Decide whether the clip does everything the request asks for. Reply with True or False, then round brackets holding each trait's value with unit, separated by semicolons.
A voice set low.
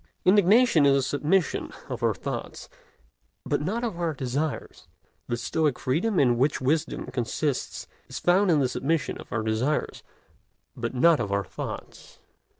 False (150 Hz)